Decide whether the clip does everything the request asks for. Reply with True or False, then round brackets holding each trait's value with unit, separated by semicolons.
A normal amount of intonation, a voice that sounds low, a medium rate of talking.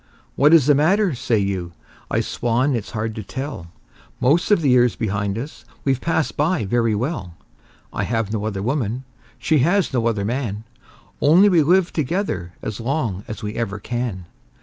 False (5.9 semitones; 120 Hz; 175 wpm)